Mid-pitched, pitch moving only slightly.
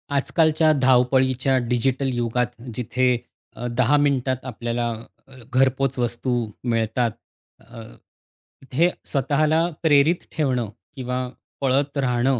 No: low, 130 Hz; narrow, 2.2 semitones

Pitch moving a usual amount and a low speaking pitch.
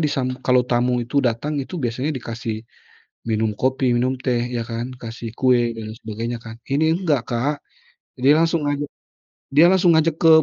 Yes: average, 3.9 semitones; low, 125 Hz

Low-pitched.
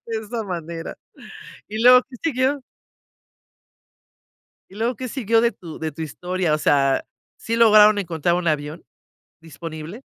No: high, 190 Hz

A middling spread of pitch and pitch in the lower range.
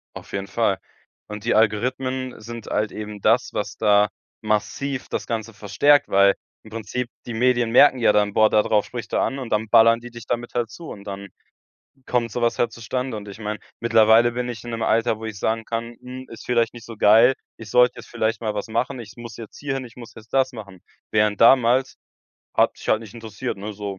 No: narrow, 2.3 semitones; low, 115 Hz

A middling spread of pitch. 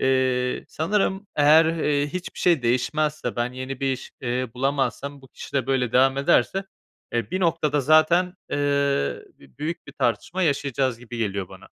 Yes: average, 3.7 semitones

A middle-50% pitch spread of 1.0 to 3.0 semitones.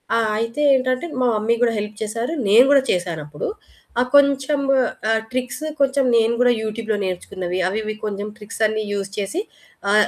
No: average, 3.7 semitones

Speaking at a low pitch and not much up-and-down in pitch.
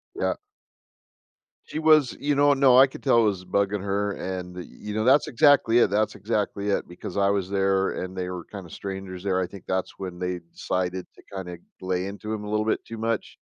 No: low, 100 Hz; average, 3.4 semitones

